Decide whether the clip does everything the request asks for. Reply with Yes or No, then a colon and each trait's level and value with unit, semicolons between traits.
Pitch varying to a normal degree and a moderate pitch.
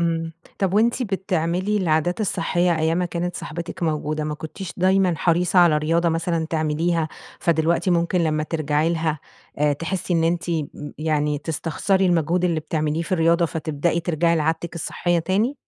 No: narrow, 2.1 semitones; medium, 170 Hz